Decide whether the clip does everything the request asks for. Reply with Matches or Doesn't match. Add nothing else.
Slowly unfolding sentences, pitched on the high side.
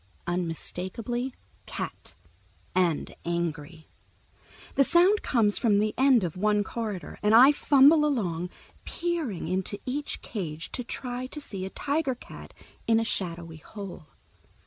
Matches